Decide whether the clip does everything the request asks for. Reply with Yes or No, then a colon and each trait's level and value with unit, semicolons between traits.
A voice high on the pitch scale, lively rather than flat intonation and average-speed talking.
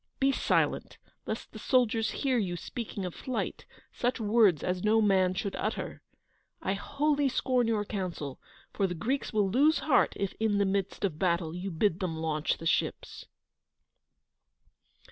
No: high, 200 Hz; average, 4.8 semitones; average, 160 wpm